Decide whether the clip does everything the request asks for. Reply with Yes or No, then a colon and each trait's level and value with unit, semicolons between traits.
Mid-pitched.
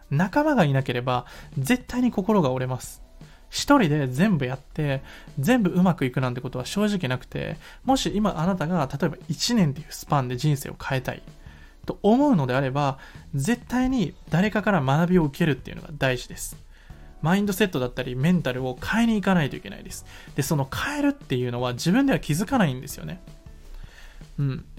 Yes: medium, 155 Hz